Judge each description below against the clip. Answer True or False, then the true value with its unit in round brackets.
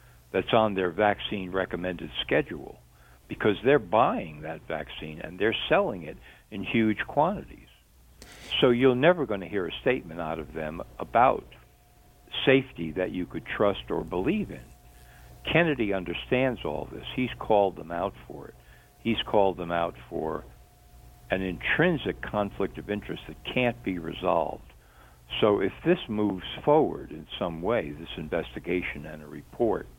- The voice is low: True (90 Hz)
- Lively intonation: True (6.3 semitones)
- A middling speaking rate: True (150 wpm)